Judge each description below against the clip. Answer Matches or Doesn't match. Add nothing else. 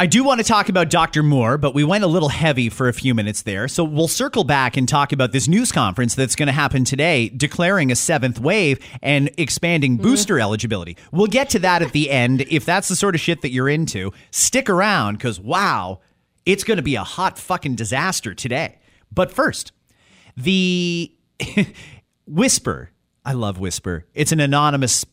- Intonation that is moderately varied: Doesn't match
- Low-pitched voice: Doesn't match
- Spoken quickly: Doesn't match